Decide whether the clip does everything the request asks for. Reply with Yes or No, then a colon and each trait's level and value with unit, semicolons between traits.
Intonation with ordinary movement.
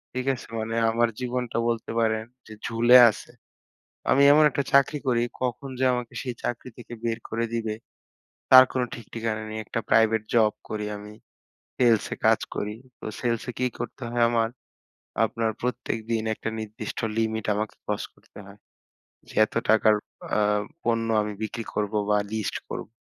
No: narrow, 1.9 semitones